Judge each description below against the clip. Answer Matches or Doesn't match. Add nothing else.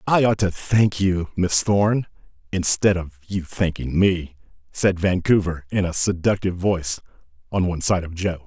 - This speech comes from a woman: Doesn't match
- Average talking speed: Matches